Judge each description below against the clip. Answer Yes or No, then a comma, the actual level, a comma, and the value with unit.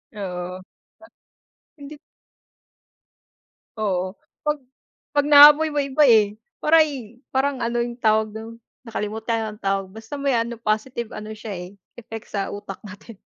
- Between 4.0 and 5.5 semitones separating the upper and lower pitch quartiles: Yes, average, 4.4 semitones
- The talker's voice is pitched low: No, high, 225 Hz